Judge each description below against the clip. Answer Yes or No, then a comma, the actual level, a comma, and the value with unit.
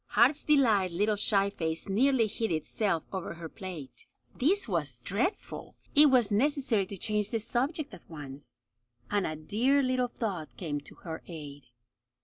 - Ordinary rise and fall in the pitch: No, wide, 7.4 semitones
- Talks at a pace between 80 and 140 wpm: No, average, 155 wpm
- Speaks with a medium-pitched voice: No, high, 200 Hz